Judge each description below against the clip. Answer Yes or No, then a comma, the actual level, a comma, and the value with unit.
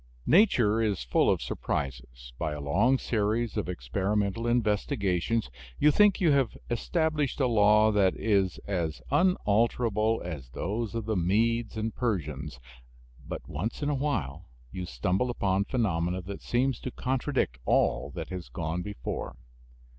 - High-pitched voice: No, low, 105 Hz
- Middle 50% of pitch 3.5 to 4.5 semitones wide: No, average, 5.1 semitones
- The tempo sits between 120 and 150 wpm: Yes, average, 145 wpm